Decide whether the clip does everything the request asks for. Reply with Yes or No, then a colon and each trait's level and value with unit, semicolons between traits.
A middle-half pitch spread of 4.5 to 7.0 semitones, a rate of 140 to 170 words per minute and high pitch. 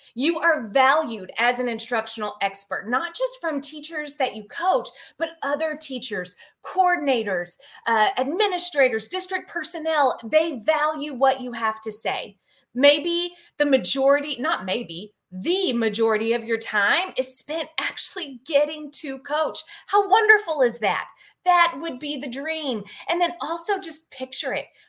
Yes: average, 5.3 semitones; average, 145 wpm; very high, 285 Hz